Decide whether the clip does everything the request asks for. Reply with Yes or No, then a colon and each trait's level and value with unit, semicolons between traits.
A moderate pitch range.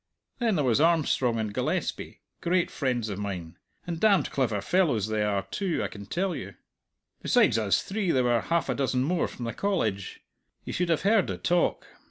No: wide, 8.5 semitones